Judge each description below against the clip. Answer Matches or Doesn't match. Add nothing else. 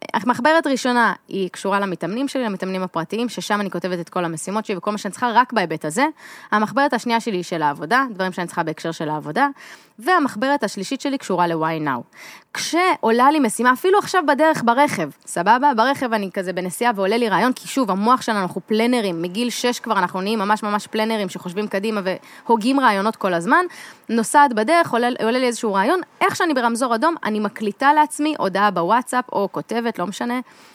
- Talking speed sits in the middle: Doesn't match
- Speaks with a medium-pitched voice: Doesn't match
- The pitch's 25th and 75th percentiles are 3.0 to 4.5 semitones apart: Doesn't match